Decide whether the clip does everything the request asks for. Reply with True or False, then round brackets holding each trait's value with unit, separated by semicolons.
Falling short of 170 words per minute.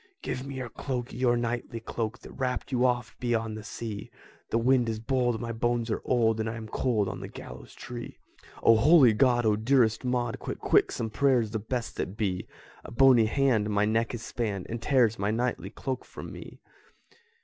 False (200 wpm)